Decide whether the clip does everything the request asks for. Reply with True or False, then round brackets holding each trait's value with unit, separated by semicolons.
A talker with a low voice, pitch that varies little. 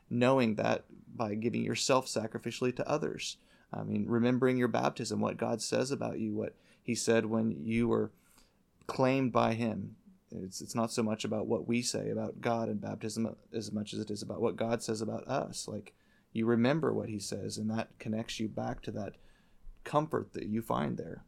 True (115 Hz; 1.5 semitones)